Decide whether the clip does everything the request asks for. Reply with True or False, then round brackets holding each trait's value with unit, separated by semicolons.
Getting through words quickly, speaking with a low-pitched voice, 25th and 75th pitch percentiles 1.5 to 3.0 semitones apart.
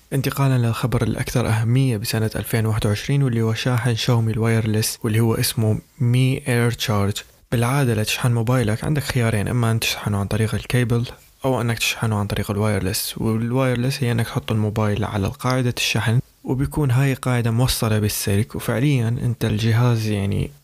True (150 wpm; 115 Hz; 2.7 semitones)